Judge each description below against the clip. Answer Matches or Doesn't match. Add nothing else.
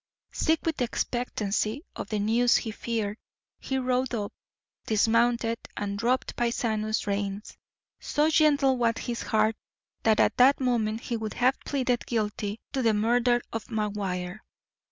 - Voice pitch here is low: Doesn't match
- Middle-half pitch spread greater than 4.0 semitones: Doesn't match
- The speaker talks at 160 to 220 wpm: Doesn't match